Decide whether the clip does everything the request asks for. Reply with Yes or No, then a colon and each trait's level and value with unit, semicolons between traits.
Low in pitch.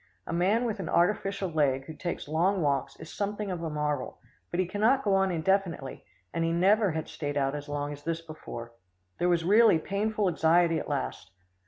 No: medium, 170 Hz